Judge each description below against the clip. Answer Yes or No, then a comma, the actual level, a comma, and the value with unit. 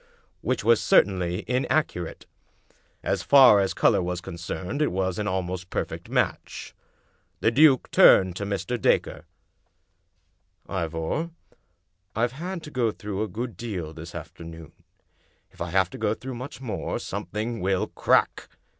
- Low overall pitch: Yes, very low, 95 Hz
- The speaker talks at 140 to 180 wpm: Yes, average, 150 wpm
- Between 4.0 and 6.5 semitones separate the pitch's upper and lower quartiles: Yes, average, 5.2 semitones